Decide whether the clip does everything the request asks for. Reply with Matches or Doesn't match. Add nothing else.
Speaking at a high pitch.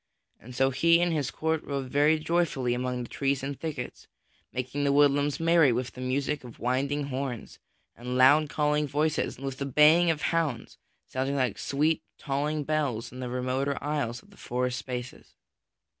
Doesn't match